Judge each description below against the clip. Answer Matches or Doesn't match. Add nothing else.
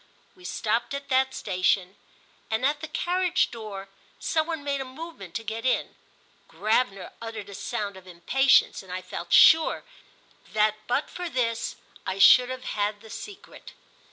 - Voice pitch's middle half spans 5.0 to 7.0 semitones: Matches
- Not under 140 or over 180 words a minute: Matches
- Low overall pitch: Doesn't match